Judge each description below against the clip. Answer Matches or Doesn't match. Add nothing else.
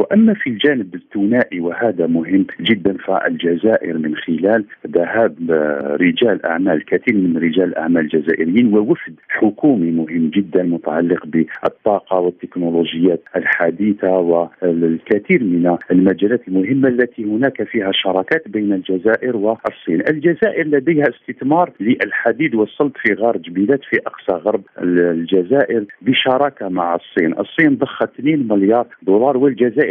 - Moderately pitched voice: Doesn't match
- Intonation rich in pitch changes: Matches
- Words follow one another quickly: Doesn't match